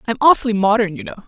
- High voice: Yes, high, 215 Hz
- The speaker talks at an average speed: No, fast, 235 wpm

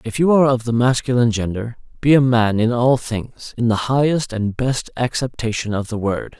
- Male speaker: Yes, male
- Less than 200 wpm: No, fast, 205 wpm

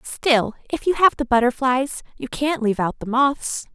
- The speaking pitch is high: Yes, very high, 260 Hz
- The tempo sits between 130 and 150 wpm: No, average, 190 wpm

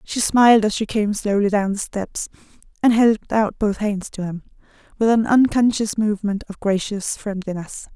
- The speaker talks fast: No, average, 175 wpm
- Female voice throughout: Yes, female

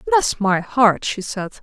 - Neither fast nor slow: Yes, average, 185 wpm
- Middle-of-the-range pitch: No, high, 215 Hz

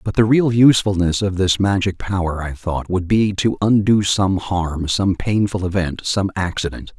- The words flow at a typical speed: Yes, average, 180 wpm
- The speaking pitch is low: Yes, very low, 95 Hz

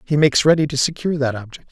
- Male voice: Yes, male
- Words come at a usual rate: No, fast, 245 wpm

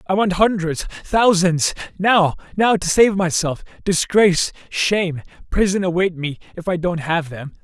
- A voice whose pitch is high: No, medium, 180 Hz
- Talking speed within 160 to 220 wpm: No, slow, 135 wpm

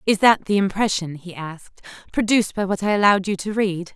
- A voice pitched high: Yes, high, 195 Hz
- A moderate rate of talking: No, fast, 215 wpm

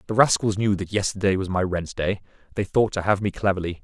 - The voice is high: No, low, 100 Hz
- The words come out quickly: Yes, fast, 235 wpm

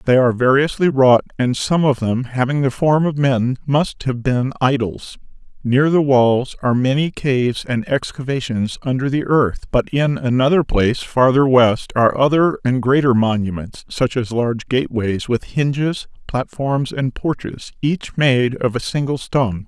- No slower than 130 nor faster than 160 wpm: No, average, 170 wpm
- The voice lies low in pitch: Yes, low, 130 Hz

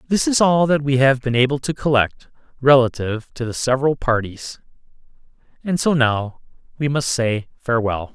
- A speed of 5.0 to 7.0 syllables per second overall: Yes, 5.1 syllables/s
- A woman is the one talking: No, male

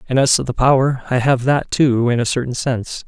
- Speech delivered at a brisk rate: Yes, fast, 255 wpm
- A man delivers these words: Yes, male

